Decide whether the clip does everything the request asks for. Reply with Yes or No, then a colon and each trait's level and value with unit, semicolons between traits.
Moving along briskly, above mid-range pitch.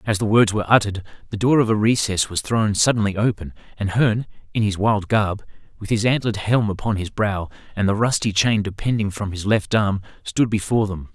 No: fast, 210 wpm; low, 105 Hz